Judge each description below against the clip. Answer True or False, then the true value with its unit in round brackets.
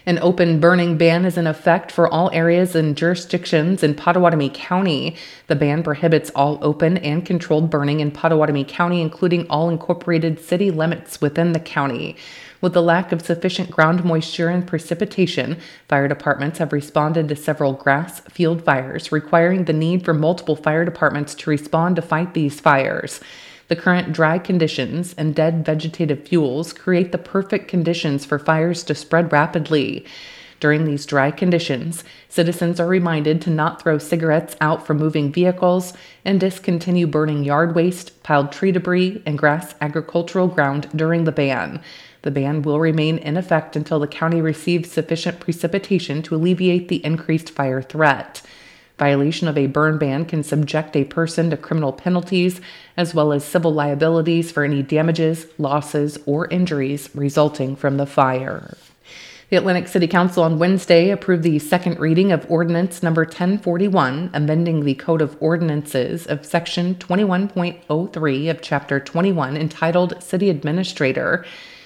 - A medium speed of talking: True (155 wpm)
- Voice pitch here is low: False (165 Hz)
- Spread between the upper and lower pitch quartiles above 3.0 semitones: False (2.6 semitones)